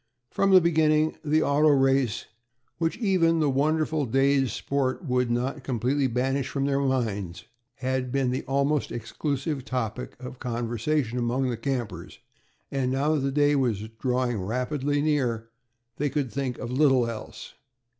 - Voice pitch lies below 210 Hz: Yes, low, 135 Hz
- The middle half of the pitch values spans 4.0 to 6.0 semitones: No, average, 2.9 semitones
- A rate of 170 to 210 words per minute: No, average, 150 wpm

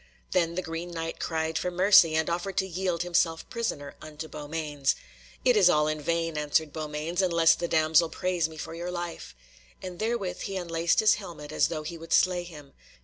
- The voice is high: No, medium, 165 Hz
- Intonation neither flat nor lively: No, narrow, 2.2 semitones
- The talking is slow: No, average, 195 wpm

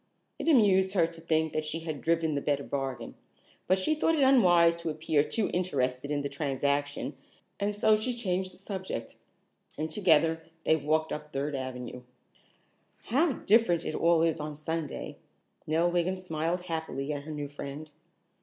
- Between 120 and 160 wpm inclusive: No, average, 170 wpm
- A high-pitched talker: No, medium, 160 Hz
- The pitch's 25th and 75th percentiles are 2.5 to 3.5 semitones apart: No, average, 4.1 semitones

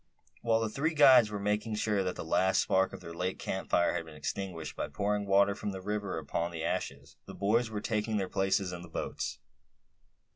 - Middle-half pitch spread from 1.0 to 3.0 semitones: Yes, average, 2.7 semitones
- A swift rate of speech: Yes, fast, 215 wpm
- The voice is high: No, low, 100 Hz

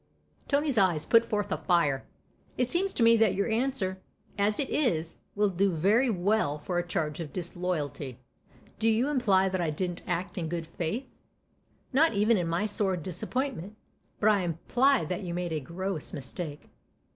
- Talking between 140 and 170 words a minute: No, average, 180 wpm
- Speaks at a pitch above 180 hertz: Yes, high, 190 Hz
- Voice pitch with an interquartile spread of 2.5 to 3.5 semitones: No, average, 4.8 semitones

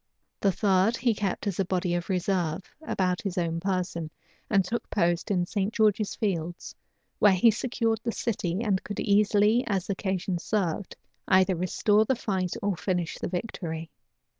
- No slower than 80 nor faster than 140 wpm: No, average, 165 wpm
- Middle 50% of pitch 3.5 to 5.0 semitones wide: No, average, 2.9 semitones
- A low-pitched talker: No, high, 190 Hz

